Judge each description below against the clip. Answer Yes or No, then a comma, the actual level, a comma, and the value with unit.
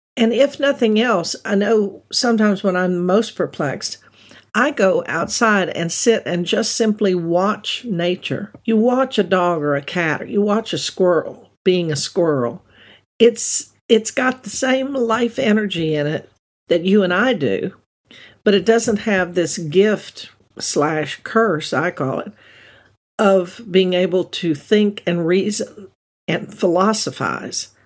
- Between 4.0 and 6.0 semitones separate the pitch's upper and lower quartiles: Yes, average, 4.3 semitones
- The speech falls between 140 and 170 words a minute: Yes, average, 150 wpm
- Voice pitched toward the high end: Yes, high, 200 Hz